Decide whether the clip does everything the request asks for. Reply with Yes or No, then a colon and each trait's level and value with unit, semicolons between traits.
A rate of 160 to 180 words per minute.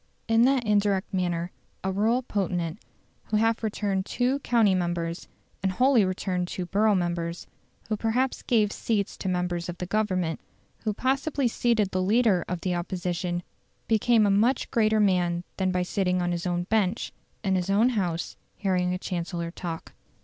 Yes: average, 165 wpm